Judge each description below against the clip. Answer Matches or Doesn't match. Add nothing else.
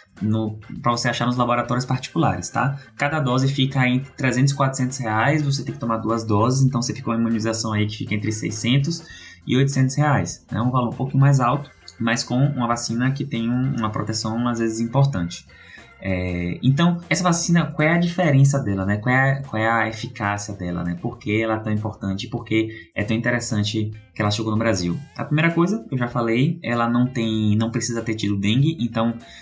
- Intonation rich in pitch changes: Doesn't match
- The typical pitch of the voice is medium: Doesn't match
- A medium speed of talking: Doesn't match